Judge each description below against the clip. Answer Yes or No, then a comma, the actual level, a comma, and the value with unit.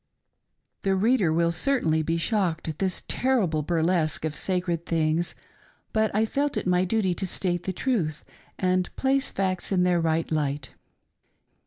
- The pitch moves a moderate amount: Yes, average, 3.4 semitones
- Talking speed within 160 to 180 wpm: Yes, average, 165 wpm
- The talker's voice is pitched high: No, medium, 180 Hz